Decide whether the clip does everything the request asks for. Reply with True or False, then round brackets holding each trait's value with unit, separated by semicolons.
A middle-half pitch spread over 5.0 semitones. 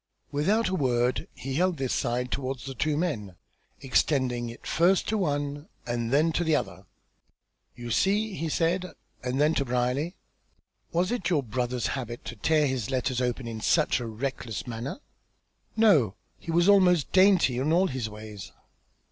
True (5.6 semitones)